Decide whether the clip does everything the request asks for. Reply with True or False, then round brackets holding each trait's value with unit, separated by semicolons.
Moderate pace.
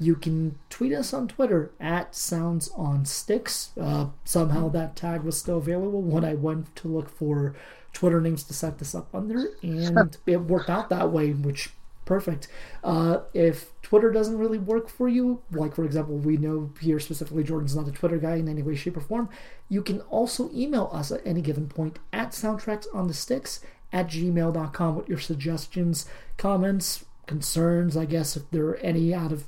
True (190 wpm)